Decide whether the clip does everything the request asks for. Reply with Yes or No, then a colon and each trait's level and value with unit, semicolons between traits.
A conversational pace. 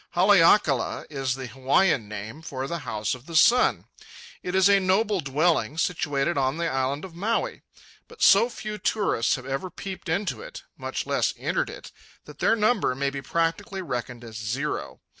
Yes: average, 175 wpm